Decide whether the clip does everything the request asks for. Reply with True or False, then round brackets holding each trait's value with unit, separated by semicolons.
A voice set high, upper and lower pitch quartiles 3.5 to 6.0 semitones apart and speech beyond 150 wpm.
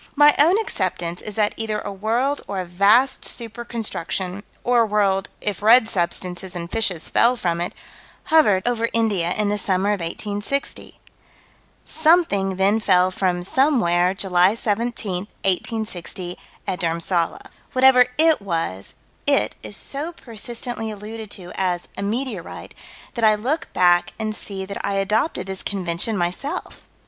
False (205 Hz; 4.1 semitones; 145 wpm)